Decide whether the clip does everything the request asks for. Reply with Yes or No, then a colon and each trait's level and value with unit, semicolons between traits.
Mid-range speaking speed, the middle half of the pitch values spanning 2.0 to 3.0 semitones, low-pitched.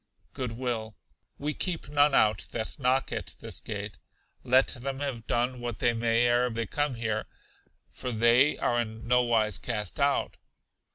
Yes: average, 165 wpm; average, 2.7 semitones; low, 120 Hz